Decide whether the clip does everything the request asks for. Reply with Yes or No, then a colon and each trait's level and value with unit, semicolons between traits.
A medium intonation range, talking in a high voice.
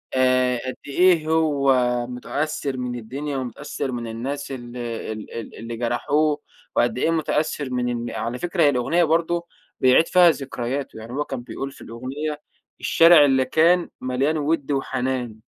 No: average, 3.8 semitones; low, 135 Hz